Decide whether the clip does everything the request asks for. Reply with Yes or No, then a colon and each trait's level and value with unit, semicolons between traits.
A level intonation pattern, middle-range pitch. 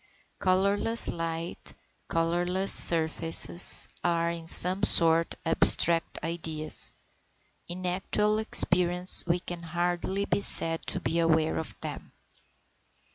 Yes: narrow, 1.8 semitones; medium, 170 Hz